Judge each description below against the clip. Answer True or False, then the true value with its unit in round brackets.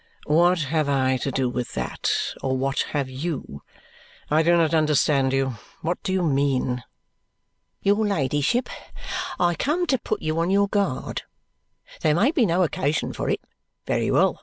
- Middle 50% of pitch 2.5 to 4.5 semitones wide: False (5.2 semitones)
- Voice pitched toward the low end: False (155 Hz)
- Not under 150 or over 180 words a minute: True (160 wpm)